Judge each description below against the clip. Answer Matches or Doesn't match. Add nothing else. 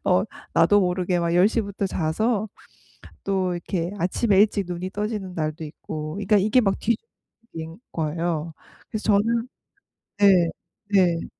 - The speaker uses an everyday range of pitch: Matches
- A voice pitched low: Doesn't match